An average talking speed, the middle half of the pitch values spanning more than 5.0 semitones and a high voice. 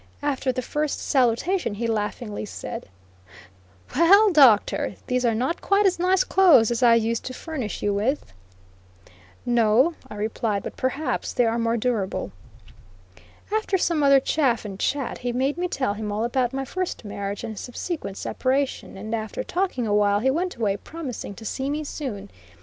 Yes: average, 165 wpm; wide, 5.4 semitones; very high, 250 Hz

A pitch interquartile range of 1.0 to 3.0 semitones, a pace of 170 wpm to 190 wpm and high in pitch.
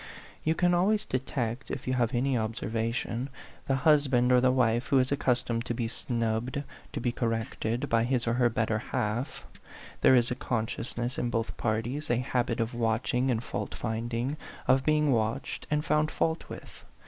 No: narrow, 2.5 semitones; average, 175 wpm; low, 120 Hz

